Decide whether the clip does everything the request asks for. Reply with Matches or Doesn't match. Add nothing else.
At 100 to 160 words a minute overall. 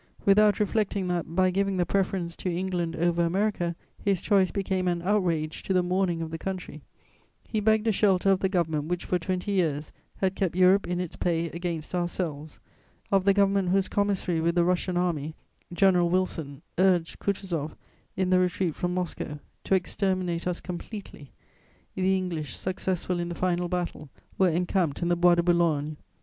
Doesn't match